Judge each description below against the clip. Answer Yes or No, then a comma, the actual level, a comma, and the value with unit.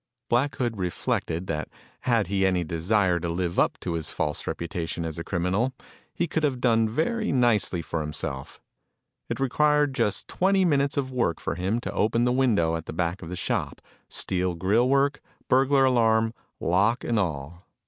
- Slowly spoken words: No, average, 180 wpm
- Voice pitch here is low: Yes, low, 105 Hz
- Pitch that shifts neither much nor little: No, wide, 7.2 semitones